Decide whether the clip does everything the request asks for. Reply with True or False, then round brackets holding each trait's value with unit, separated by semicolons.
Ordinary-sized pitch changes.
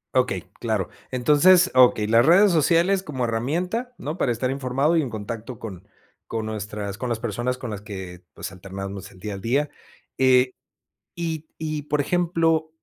False (6.7 semitones)